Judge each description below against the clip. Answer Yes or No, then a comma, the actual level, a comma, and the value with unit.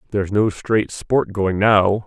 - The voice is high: No, low, 105 Hz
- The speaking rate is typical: Yes, average, 175 wpm